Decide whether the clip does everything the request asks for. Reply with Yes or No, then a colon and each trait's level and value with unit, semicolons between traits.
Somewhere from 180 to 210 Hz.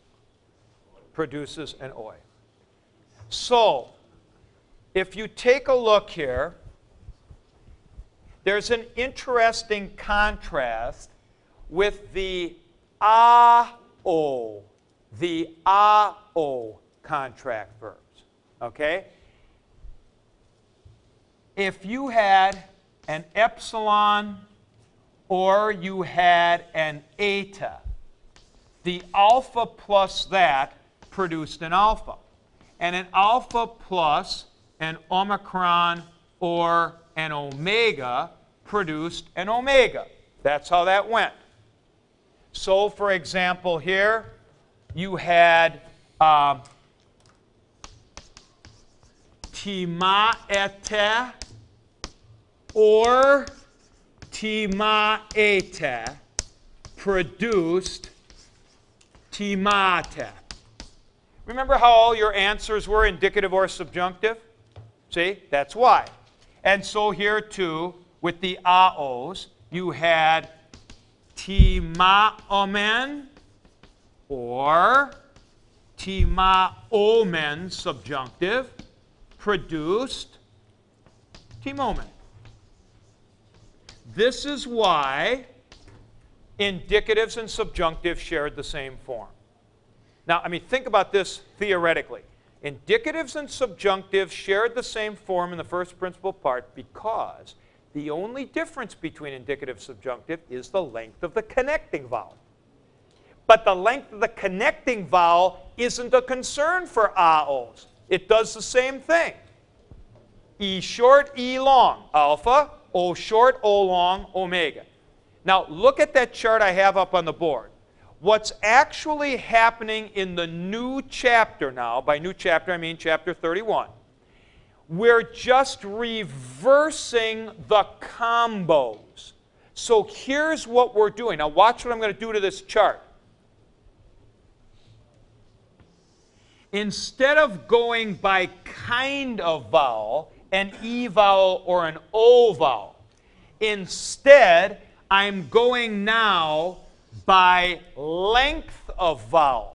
Yes: high, 190 Hz